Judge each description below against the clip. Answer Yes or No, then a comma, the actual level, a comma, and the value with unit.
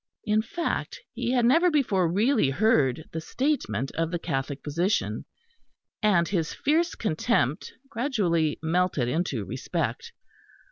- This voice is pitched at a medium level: Yes, medium, 180 Hz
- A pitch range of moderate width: No, wide, 7.3 semitones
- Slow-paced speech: Yes, slow, 125 wpm